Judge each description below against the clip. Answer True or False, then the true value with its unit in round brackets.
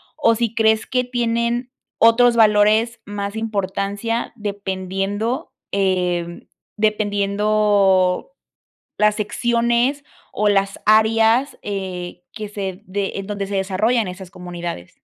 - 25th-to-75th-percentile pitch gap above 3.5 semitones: False (2.8 semitones)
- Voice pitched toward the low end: False (210 Hz)